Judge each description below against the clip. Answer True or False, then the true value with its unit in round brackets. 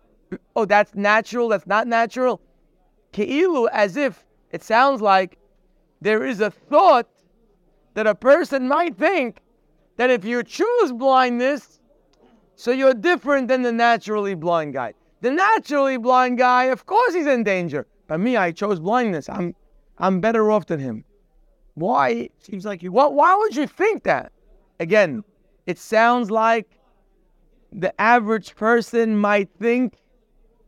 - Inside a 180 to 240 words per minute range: False (140 wpm)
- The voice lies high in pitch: True (225 Hz)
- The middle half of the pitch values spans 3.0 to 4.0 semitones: False (4.6 semitones)